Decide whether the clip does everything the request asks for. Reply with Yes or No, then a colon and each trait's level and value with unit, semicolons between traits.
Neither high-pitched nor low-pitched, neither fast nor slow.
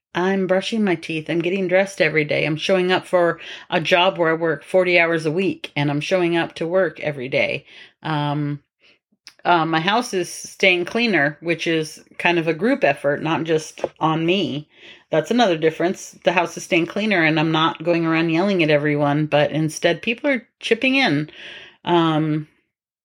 Yes: medium, 170 Hz; average, 185 wpm